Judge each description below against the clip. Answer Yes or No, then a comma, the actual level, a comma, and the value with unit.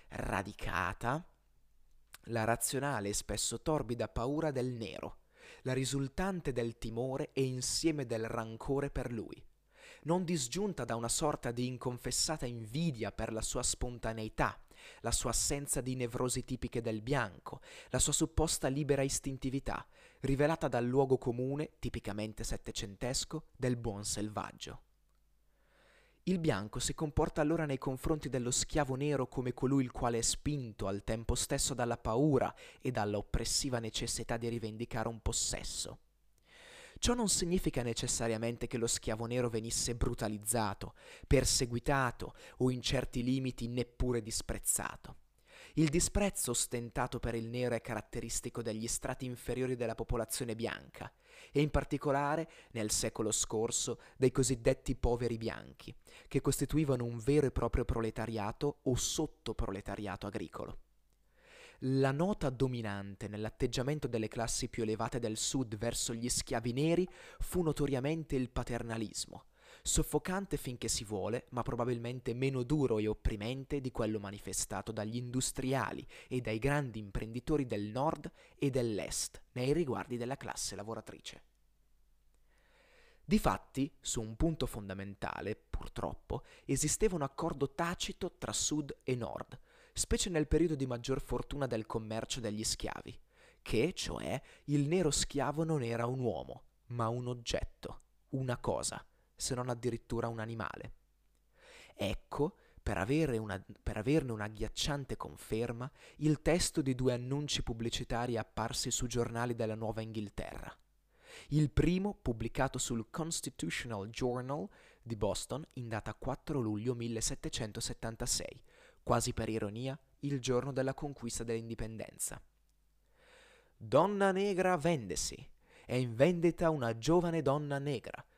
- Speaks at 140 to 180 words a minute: No, average, 130 wpm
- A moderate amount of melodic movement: Yes, average, 3.8 semitones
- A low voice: Yes, low, 125 Hz